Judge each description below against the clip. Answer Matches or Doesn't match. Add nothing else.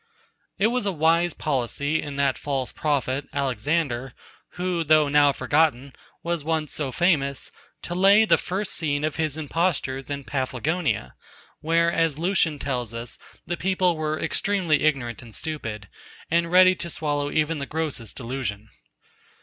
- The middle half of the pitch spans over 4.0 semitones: Doesn't match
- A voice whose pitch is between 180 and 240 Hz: Doesn't match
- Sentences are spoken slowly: Doesn't match